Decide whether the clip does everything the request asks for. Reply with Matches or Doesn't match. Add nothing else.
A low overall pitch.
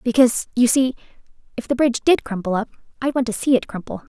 Doesn't match